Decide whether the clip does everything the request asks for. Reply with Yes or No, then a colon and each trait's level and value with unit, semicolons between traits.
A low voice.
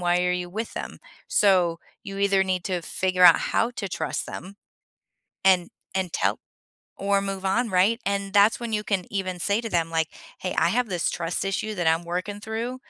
No: high, 190 Hz